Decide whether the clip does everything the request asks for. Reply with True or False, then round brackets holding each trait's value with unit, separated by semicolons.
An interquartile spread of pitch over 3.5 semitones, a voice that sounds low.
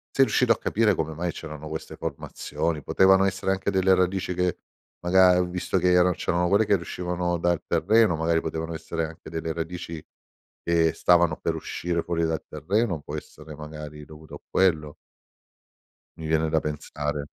False (2.4 semitones; 85 Hz)